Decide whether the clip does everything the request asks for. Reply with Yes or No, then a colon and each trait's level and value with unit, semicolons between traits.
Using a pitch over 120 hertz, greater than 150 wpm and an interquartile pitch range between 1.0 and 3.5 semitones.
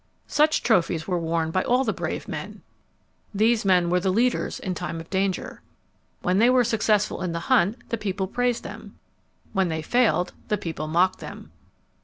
No: high, 190 Hz; average, 180 wpm; average, 4.6 semitones